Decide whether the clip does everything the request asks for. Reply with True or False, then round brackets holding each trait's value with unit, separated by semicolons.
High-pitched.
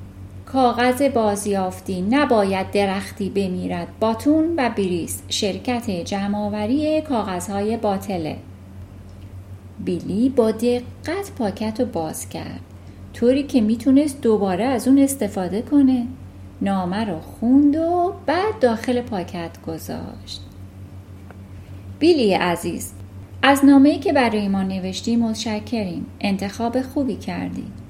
True (205 Hz)